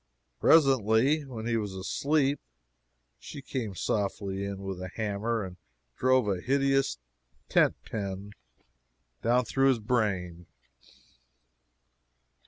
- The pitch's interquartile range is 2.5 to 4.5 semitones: No, average, 5.2 semitones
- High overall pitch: No, low, 110 Hz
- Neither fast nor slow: No, slow, 105 wpm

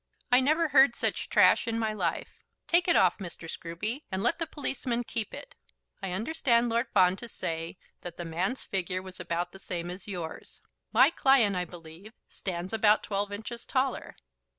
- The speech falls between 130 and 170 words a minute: No, average, 180 wpm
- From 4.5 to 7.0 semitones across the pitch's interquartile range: Yes, average, 5.3 semitones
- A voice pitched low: No, high, 205 Hz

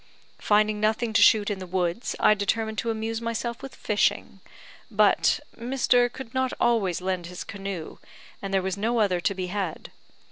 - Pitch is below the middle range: No, high, 210 Hz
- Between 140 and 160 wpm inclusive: No, average, 175 wpm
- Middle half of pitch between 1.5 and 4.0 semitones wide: Yes, average, 3.3 semitones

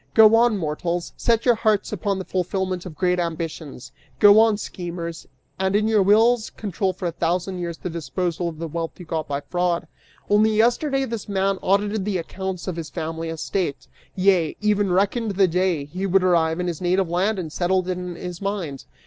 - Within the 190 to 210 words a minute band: Yes, average, 195 wpm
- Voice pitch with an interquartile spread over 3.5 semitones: No, average, 3.2 semitones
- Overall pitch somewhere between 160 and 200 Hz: Yes, medium, 185 Hz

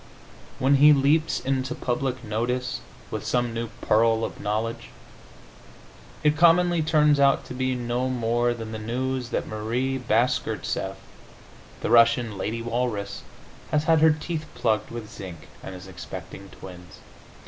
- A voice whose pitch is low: Yes, low, 120 Hz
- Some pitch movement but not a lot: Yes, average, 3.5 semitones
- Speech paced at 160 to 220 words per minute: No, average, 140 wpm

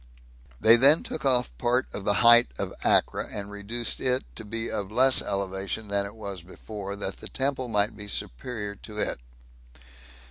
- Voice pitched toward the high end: No, low, 105 Hz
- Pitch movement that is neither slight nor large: Yes, average, 3.2 semitones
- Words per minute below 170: No, average, 175 wpm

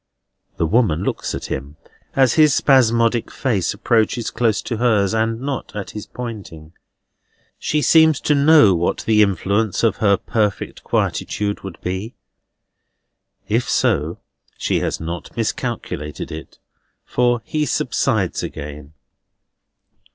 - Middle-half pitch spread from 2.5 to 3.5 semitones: No, average, 4.8 semitones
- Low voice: Yes, low, 110 Hz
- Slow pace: Yes, slow, 125 wpm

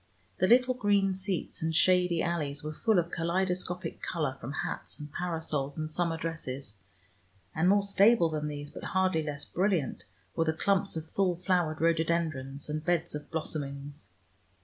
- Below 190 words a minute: Yes, average, 160 wpm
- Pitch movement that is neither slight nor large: Yes, average, 3.5 semitones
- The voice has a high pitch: No, medium, 165 Hz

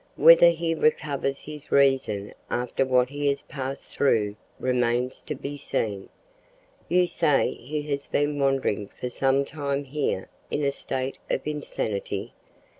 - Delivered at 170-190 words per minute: No, average, 140 wpm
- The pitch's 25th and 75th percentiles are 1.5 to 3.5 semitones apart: Yes, average, 2.8 semitones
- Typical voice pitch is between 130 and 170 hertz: Yes, medium, 140 Hz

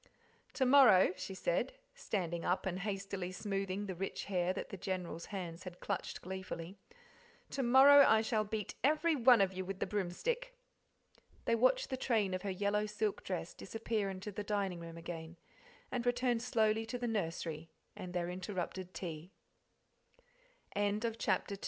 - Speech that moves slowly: No, average, 170 wpm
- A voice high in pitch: Yes, high, 200 Hz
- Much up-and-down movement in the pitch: No, average, 3.6 semitones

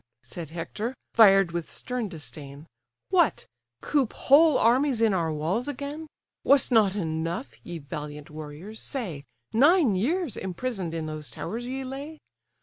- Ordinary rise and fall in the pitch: No, wide, 8.6 semitones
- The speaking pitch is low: No, high, 205 Hz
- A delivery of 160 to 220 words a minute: No, average, 140 wpm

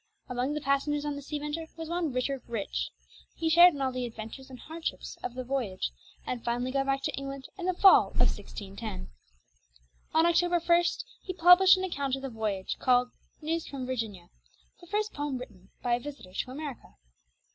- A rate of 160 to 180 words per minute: No, average, 190 wpm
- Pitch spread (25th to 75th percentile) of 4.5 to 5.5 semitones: Yes, average, 4.8 semitones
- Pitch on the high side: Yes, very high, 275 Hz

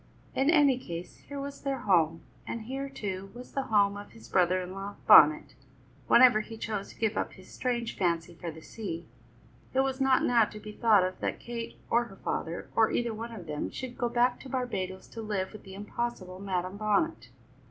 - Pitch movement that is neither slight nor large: Yes, average, 4.6 semitones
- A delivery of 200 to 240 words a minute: Yes, fast, 205 wpm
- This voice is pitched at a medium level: No, high, 215 Hz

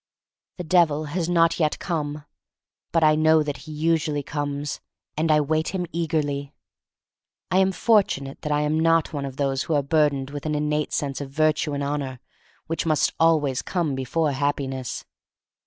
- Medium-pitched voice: Yes, medium, 150 Hz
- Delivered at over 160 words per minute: Yes, average, 170 wpm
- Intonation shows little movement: Yes, narrow, 2.2 semitones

